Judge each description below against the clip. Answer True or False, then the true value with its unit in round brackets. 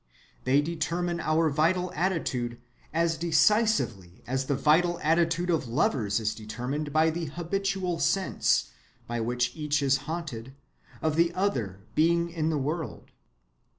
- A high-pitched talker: False (155 Hz)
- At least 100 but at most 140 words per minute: True (135 wpm)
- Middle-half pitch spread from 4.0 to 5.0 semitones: True (4.5 semitones)